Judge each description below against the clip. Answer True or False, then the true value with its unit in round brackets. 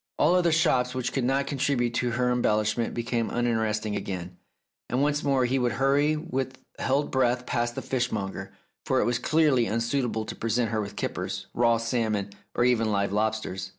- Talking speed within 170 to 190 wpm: True (185 wpm)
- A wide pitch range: False (3.2 semitones)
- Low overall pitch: True (120 Hz)